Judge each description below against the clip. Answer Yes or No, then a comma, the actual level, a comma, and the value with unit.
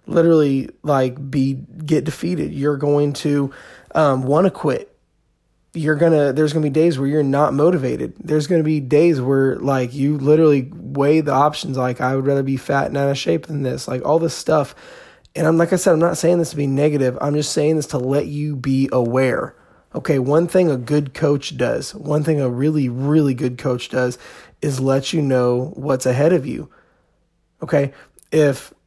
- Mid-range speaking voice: Yes, medium, 145 Hz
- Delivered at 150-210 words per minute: Yes, fast, 205 wpm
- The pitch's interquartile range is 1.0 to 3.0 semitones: Yes, narrow, 2.6 semitones